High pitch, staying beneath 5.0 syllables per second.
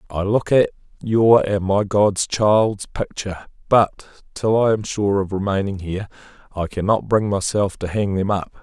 No: low, 100 Hz; 4.5 syllables/s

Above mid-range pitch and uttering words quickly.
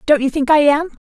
Yes: very high, 295 Hz; fast, 280 wpm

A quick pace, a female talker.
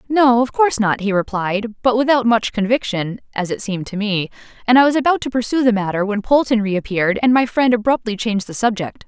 Yes: fast, 220 wpm; female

